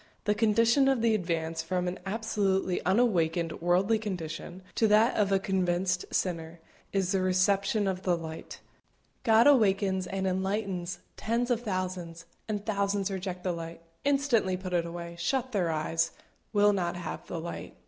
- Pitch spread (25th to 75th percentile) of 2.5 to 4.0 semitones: Yes, average, 3.3 semitones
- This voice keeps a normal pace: Yes, average, 160 wpm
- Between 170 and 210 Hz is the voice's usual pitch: Yes, high, 190 Hz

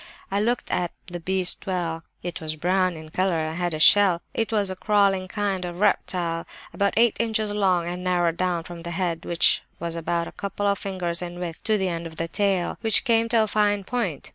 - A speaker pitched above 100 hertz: Yes, medium, 185 Hz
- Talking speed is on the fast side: Yes, fast, 220 wpm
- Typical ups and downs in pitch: Yes, average, 3.1 semitones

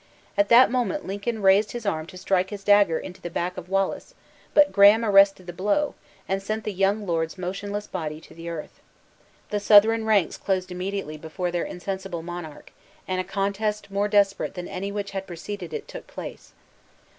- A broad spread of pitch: No, narrow, 2.4 semitones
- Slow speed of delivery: No, average, 185 wpm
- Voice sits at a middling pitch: No, high, 195 Hz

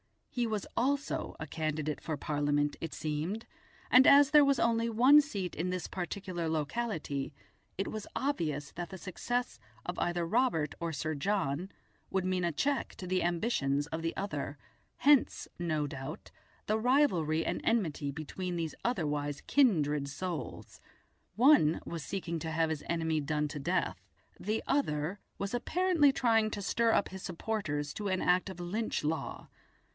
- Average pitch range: No, wide, 6.5 semitones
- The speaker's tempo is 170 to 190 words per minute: No, average, 160 wpm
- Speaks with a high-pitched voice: No, medium, 175 Hz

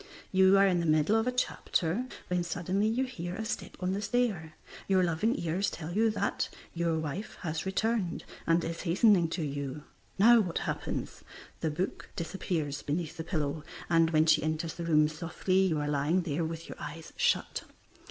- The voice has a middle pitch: Yes, medium, 170 Hz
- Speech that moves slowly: No, average, 185 wpm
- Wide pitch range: No, average, 3.4 semitones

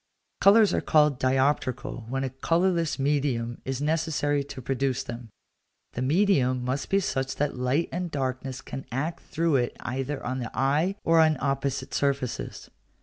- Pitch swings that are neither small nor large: Yes, average, 3.2 semitones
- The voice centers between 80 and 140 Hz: Yes, low, 135 Hz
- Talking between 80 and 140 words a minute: No, average, 155 wpm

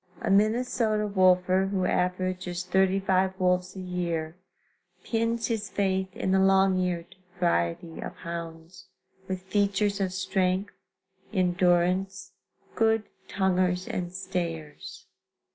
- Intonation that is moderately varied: No, narrow, 1.3 semitones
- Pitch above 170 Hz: Yes, medium, 185 Hz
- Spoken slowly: Yes, slow, 110 wpm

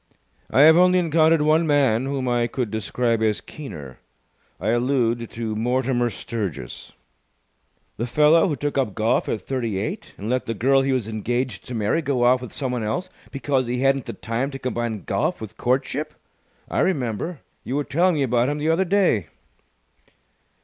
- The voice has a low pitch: Yes, low, 125 Hz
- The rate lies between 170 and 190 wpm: Yes, average, 175 wpm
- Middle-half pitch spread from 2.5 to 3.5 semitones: No, average, 4.1 semitones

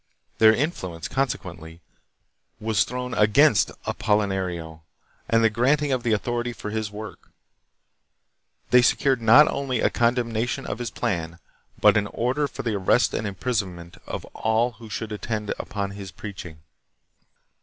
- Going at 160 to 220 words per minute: No, average, 140 wpm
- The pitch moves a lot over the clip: No, average, 3.6 semitones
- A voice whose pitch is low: Yes, low, 110 Hz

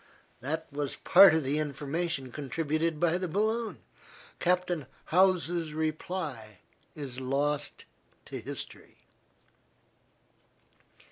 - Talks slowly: Yes, slow, 90 wpm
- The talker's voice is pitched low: No, medium, 155 Hz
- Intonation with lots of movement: No, average, 3.6 semitones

